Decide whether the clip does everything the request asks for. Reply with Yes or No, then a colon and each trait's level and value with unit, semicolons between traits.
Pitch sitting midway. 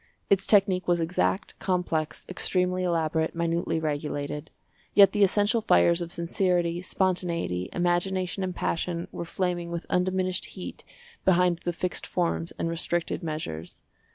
Yes: medium, 175 Hz